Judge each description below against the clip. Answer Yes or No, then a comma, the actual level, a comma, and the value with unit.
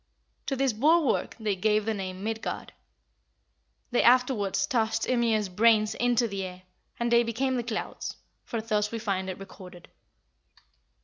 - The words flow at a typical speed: Yes, average, 150 wpm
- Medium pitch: No, high, 220 Hz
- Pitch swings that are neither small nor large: Yes, average, 3.3 semitones